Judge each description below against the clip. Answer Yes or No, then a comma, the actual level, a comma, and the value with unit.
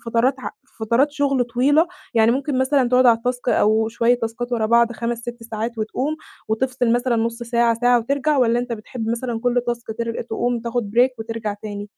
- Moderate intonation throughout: No, narrow, 1.7 semitones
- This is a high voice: Yes, high, 235 Hz